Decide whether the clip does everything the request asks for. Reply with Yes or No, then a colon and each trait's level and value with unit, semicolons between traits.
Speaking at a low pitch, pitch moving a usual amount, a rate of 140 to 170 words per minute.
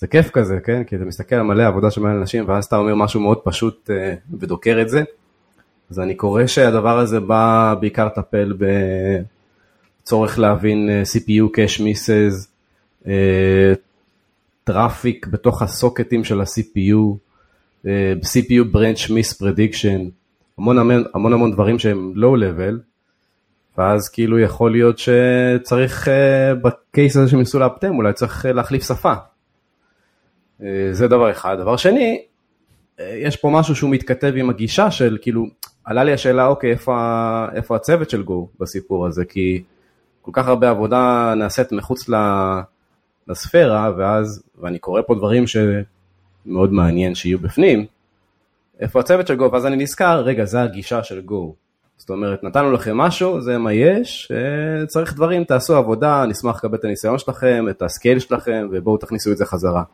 Yes: low, 110 Hz; average, 3.8 semitones; average, 145 wpm